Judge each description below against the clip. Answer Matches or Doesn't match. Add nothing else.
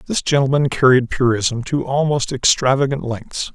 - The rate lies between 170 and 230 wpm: Doesn't match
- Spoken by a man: Matches